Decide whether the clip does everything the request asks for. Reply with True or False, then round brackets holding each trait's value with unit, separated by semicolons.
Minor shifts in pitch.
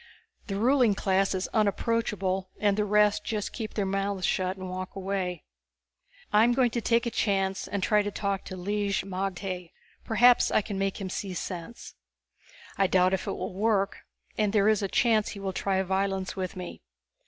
True (1.8 semitones)